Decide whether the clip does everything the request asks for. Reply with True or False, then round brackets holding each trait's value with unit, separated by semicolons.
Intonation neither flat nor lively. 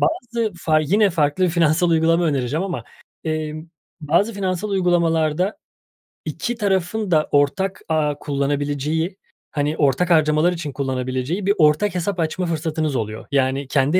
True (3.9 semitones)